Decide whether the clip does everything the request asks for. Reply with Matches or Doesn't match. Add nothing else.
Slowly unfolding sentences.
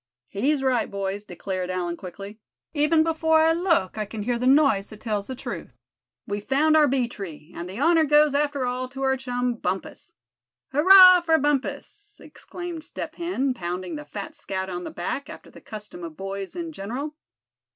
Doesn't match